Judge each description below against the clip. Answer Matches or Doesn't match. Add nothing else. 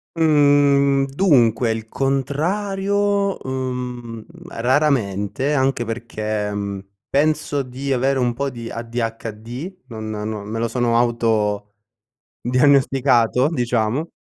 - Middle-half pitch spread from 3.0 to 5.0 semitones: Matches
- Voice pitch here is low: Matches